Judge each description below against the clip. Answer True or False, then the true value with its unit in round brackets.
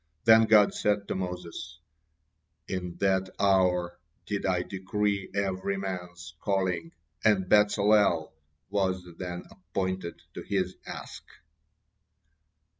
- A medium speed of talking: False (105 wpm)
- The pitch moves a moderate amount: False (1.9 semitones)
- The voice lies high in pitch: False (95 Hz)